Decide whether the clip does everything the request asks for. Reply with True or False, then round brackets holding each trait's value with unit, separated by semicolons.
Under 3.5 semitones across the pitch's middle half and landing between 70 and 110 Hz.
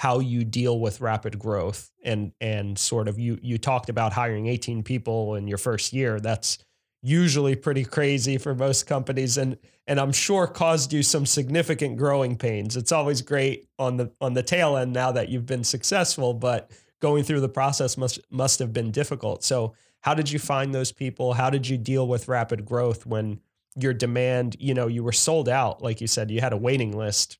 False (3.0 semitones; 125 Hz)